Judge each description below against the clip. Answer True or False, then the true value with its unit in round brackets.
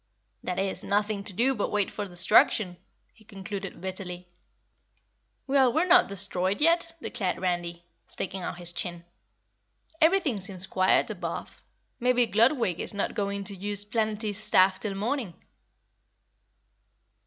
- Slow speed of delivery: True (130 wpm)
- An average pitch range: True (3.5 semitones)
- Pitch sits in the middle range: False (200 Hz)